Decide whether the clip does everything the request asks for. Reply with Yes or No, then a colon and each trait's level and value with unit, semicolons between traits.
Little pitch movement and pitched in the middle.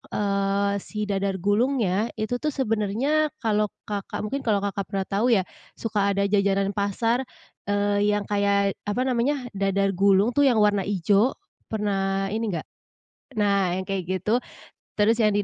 No: narrow, 2.2 semitones; high, 205 Hz